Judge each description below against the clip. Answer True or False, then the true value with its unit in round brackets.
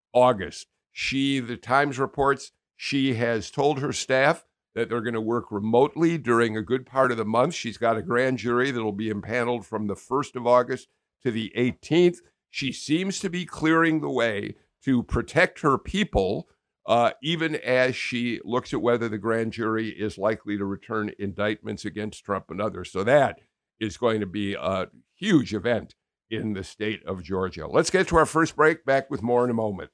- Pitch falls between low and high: False (120 Hz)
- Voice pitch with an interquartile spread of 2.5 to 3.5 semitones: False (4.2 semitones)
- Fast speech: False (190 wpm)